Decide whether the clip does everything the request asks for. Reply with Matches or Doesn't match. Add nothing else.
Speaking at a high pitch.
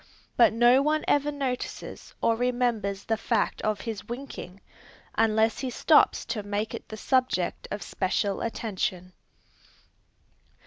Matches